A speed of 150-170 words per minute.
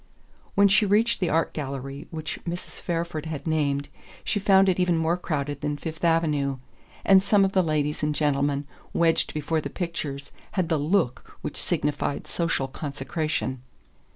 Yes: average, 160 wpm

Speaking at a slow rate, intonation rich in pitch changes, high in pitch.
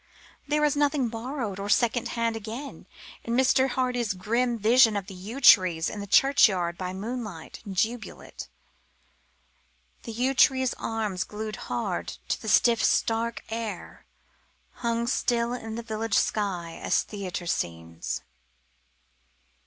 No: slow, 130 wpm; average, 3.7 semitones; high, 225 Hz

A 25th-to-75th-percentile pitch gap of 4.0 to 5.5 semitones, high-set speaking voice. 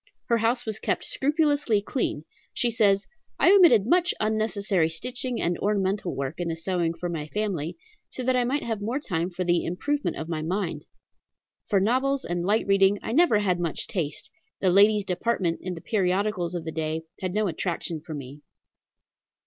Yes: average, 5.0 semitones; high, 195 Hz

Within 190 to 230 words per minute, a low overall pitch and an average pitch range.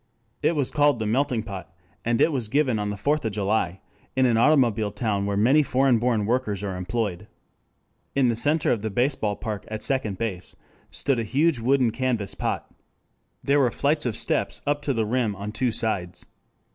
Yes: average, 195 wpm; low, 115 Hz; average, 4.5 semitones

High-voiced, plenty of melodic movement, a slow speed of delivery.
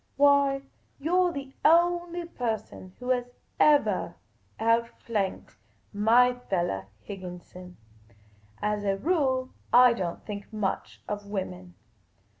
Yes: high, 230 Hz; wide, 6.1 semitones; slow, 110 wpm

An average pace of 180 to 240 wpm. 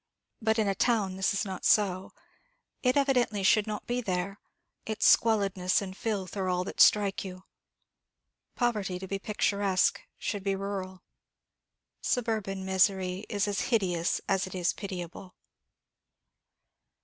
No: slow, 135 wpm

